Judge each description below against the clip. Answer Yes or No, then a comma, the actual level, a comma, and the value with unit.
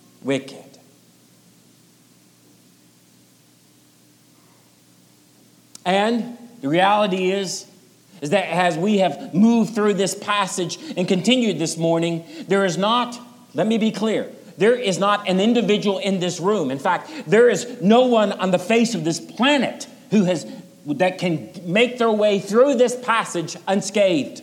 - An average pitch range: No, wide, 7.8 semitones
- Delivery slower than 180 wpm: Yes, average, 140 wpm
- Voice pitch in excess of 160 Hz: Yes, high, 190 Hz